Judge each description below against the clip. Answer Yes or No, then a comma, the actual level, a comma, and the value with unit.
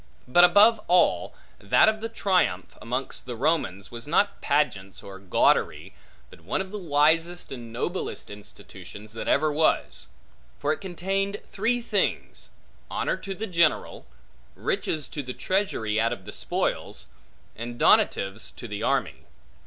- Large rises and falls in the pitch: Yes, wide, 9.0 semitones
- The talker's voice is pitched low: No, medium, 150 Hz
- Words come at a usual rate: Yes, average, 145 wpm